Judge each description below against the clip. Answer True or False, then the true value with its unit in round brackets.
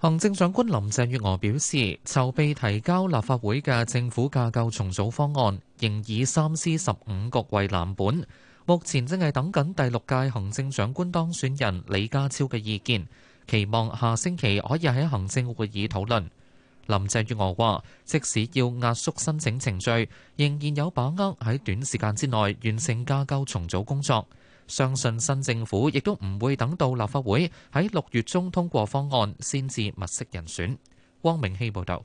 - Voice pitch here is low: True (125 Hz)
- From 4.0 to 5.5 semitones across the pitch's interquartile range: True (4.8 semitones)